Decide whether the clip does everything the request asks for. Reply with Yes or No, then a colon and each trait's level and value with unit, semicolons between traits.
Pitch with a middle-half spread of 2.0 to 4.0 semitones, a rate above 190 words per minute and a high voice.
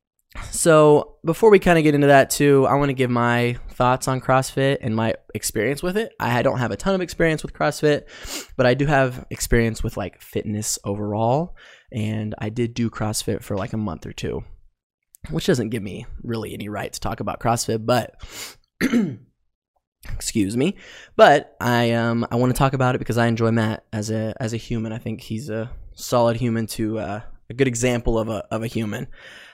No: average, 3.4 semitones; average, 200 wpm; low, 115 Hz